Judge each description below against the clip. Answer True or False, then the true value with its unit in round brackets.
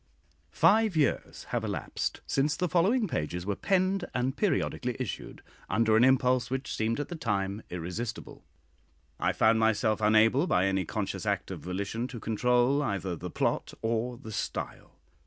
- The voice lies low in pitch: True (120 Hz)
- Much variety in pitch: False (5.0 semitones)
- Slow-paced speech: False (155 wpm)